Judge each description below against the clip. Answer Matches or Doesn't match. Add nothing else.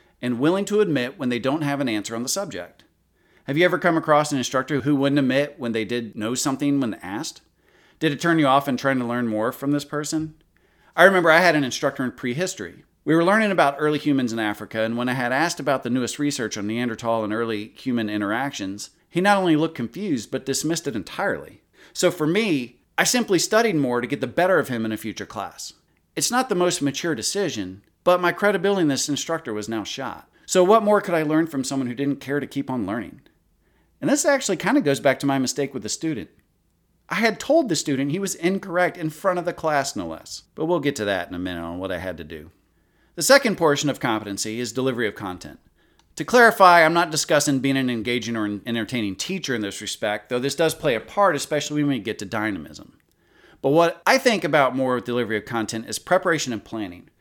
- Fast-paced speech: Matches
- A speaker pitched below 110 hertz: Doesn't match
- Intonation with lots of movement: Matches